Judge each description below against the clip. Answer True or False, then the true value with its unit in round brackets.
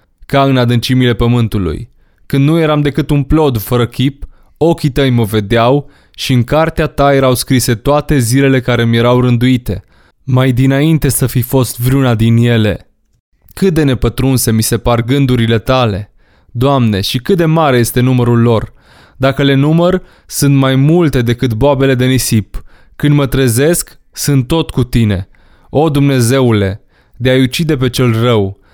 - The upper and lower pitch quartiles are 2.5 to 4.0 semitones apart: True (3.1 semitones)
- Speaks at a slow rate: False (160 wpm)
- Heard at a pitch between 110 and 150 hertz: True (130 Hz)